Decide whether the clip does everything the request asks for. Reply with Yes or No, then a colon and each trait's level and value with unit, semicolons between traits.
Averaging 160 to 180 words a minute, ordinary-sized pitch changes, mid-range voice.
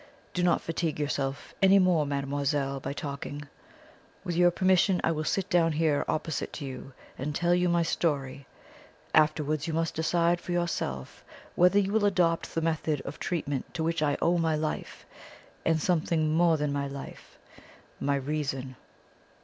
Yes: average, 165 wpm; average, 3.3 semitones; medium, 155 Hz